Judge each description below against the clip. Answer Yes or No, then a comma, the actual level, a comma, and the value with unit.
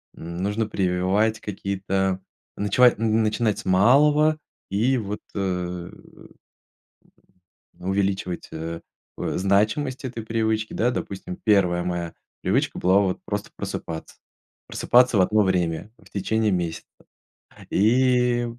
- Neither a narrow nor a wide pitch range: Yes, average, 3.6 semitones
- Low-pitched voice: Yes, low, 100 Hz